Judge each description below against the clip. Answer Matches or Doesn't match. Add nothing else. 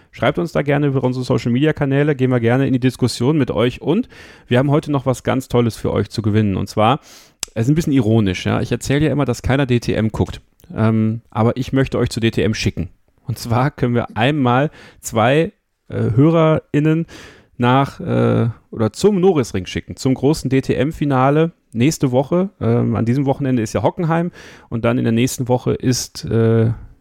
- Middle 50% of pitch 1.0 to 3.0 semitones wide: Doesn't match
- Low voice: Matches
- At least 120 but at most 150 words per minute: Doesn't match